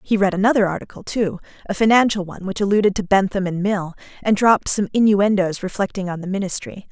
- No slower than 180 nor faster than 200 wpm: Yes, average, 190 wpm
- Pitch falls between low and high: No, high, 195 Hz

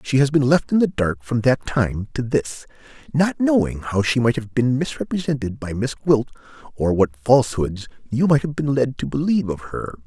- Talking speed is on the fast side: Yes, fast, 210 wpm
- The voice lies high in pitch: No, low, 125 Hz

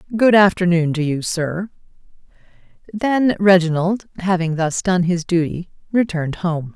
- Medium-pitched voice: Yes, medium, 180 Hz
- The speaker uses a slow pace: Yes, slow, 125 wpm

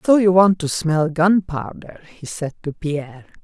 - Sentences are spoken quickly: No, average, 175 wpm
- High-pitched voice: No, medium, 170 Hz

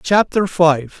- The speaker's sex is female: No, male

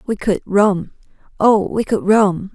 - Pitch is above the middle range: Yes, high, 205 Hz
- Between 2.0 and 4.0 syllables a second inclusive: Yes, 3.7 syllables/s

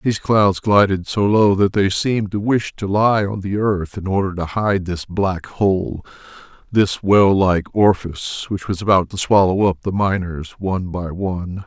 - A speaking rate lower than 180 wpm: No, average, 190 wpm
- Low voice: Yes, very low, 95 Hz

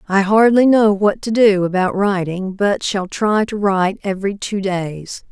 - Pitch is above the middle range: Yes, high, 200 Hz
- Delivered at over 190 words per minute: No, average, 180 wpm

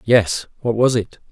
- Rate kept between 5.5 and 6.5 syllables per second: No, 4.0 syllables/s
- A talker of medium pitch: No, low, 115 Hz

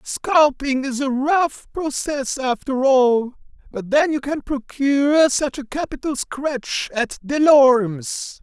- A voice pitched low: No, very high, 270 Hz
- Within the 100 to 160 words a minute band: Yes, slow, 135 wpm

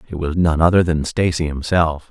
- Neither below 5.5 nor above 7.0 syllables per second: No, 5.1 syllables/s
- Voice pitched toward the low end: Yes, very low, 80 Hz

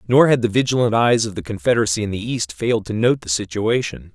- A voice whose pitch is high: No, low, 110 Hz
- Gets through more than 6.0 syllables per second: Yes, 6.3 syllables/s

